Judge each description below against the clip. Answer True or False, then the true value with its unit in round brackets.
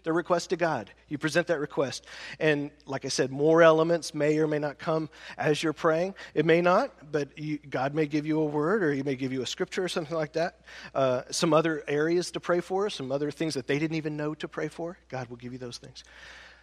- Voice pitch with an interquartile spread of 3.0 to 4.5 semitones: False (2.4 semitones)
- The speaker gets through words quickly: True (245 wpm)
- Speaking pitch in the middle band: True (155 Hz)